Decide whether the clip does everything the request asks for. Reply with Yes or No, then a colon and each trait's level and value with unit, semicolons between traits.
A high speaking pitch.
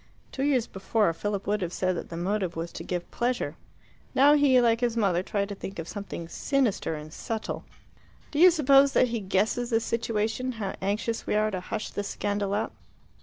Yes: high, 210 Hz